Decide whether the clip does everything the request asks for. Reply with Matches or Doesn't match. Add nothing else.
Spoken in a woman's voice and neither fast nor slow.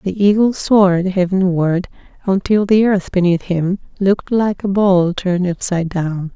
Matches